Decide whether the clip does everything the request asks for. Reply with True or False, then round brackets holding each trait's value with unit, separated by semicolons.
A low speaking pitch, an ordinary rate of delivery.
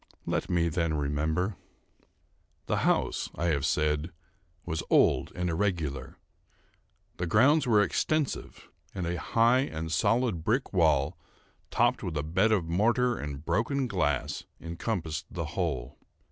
False (85 Hz; 130 wpm)